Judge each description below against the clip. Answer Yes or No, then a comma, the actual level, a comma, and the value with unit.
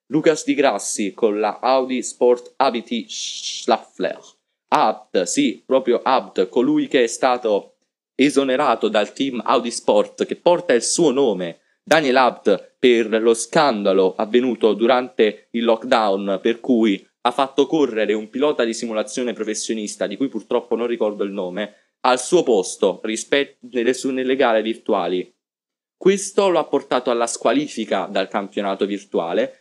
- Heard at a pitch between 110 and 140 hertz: Yes, low, 125 Hz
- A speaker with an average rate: Yes, average, 140 wpm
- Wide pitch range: No, average, 5.0 semitones